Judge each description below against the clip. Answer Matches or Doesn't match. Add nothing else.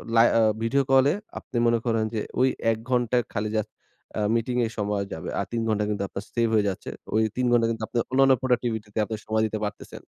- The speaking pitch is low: Matches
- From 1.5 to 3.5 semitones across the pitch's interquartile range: Matches